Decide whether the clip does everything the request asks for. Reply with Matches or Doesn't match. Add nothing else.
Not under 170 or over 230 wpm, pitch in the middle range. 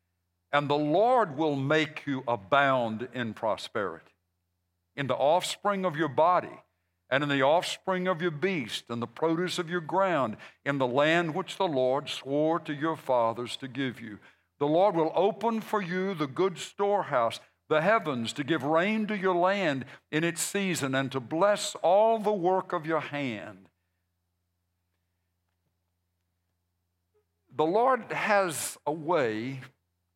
Doesn't match